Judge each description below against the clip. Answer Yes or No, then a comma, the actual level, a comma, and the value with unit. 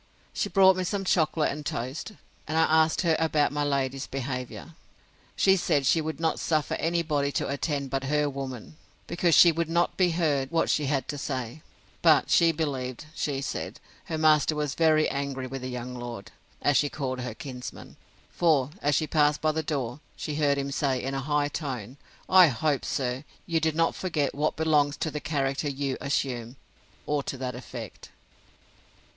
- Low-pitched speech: No, medium, 145 Hz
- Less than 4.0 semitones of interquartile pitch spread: Yes, average, 2.9 semitones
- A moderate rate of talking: Yes, average, 185 wpm